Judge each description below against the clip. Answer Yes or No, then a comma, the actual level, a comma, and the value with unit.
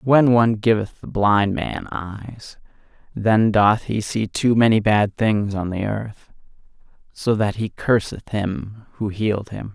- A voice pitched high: No, low, 105 Hz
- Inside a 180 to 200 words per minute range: No, average, 165 wpm